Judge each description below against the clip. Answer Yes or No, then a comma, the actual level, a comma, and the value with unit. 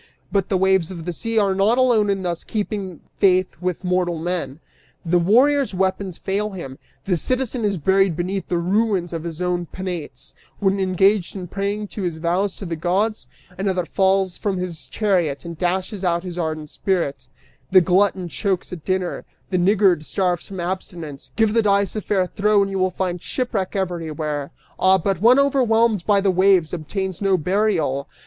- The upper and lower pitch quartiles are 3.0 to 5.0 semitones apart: No, narrow, 2.5 semitones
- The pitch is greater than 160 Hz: Yes, high, 190 Hz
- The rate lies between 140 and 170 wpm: No, average, 180 wpm